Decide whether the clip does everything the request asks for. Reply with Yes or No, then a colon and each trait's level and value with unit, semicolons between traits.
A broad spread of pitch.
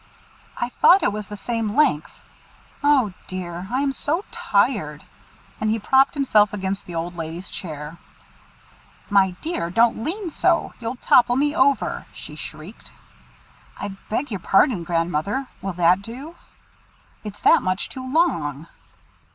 Yes: wide, 6.9 semitones